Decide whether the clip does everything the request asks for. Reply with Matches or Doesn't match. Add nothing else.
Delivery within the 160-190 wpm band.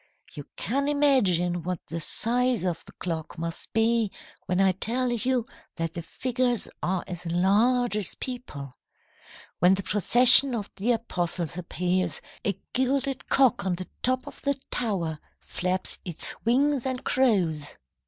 Doesn't match